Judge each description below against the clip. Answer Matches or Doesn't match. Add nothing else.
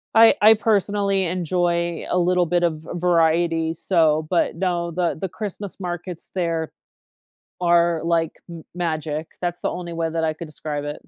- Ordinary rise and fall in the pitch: Doesn't match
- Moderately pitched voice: Matches